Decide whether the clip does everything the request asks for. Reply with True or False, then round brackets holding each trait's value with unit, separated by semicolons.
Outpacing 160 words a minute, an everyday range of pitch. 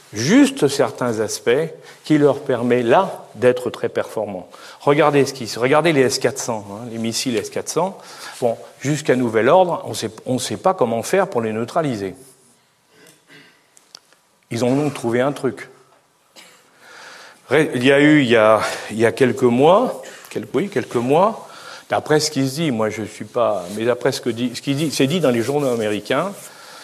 True (180 wpm; 4.2 semitones)